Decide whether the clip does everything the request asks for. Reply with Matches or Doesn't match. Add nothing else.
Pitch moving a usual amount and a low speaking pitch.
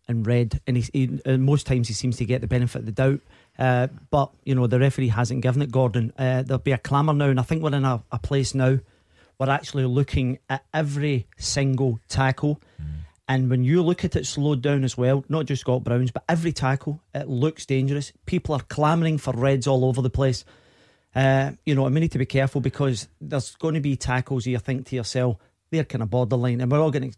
Doesn't match